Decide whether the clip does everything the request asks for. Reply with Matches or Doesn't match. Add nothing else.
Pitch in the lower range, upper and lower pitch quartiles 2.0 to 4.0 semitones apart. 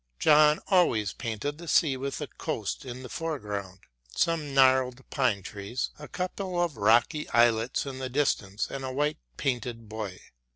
Doesn't match